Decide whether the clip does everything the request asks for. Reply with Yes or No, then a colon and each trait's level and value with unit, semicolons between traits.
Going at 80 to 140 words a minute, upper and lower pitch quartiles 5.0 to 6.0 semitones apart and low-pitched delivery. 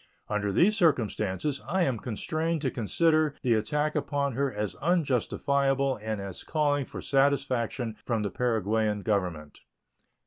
Yes: slow, 135 wpm; wide, 5.4 semitones; low, 130 Hz